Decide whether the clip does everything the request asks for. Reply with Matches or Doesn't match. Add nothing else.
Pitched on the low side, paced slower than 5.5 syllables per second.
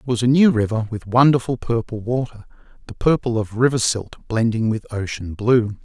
Matches